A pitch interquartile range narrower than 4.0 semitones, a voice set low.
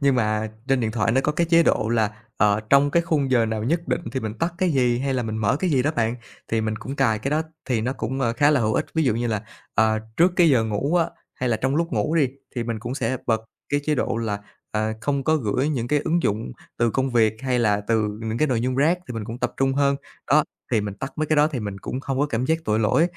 No: average, 4.5 semitones; low, 125 Hz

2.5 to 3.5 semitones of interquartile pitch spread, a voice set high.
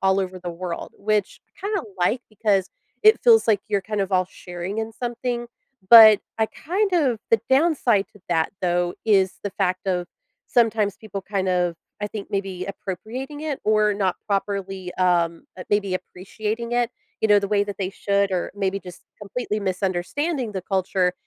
Yes: average, 3.2 semitones; high, 200 Hz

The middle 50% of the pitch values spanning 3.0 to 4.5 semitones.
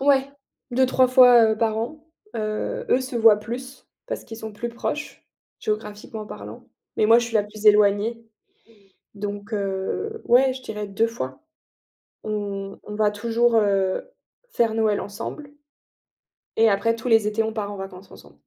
No: narrow, 2.4 semitones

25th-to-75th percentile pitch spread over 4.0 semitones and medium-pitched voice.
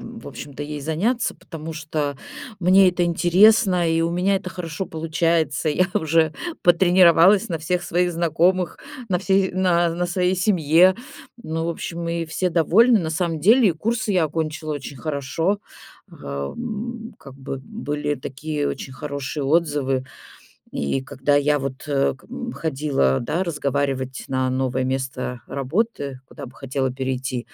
Yes: average, 4.4 semitones; medium, 160 Hz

